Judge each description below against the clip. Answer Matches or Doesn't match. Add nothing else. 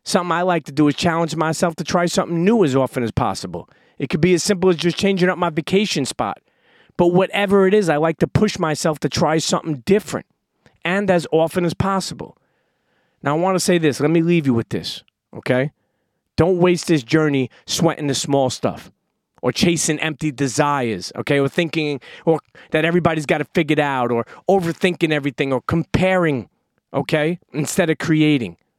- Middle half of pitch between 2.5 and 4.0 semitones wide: Matches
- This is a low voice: Doesn't match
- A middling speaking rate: Matches